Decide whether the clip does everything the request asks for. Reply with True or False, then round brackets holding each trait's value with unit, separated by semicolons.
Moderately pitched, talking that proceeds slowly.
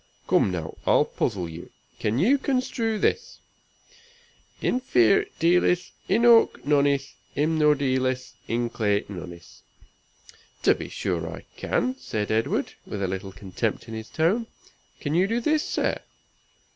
False (130 Hz; 130 wpm)